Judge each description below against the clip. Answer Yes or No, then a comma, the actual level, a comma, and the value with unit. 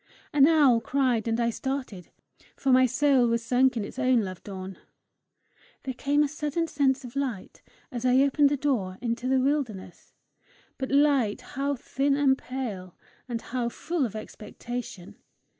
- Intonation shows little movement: No, average, 3.3 semitones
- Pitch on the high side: Yes, very high, 255 Hz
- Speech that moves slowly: No, average, 160 wpm